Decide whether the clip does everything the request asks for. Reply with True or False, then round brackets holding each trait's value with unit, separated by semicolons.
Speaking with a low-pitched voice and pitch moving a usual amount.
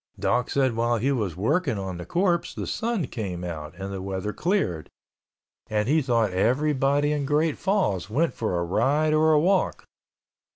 False (125 Hz; 8.0 semitones)